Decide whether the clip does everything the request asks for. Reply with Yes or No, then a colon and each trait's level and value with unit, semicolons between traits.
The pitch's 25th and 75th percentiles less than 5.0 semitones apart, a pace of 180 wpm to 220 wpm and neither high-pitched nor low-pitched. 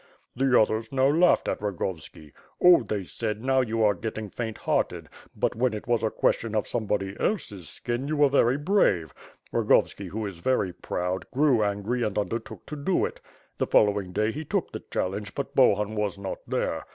No: average, 4.3 semitones; average, 190 wpm; low, 110 Hz